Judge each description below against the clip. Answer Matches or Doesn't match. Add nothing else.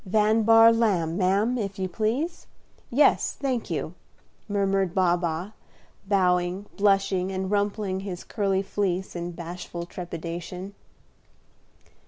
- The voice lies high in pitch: Matches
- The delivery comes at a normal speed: Doesn't match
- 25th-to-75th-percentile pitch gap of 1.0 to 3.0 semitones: Matches